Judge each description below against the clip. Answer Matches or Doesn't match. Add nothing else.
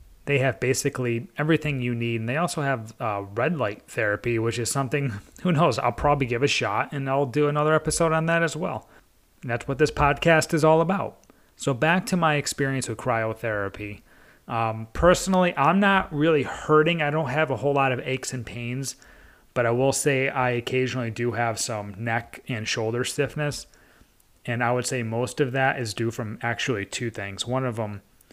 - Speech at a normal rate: Matches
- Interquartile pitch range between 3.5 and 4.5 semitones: Matches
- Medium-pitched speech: Doesn't match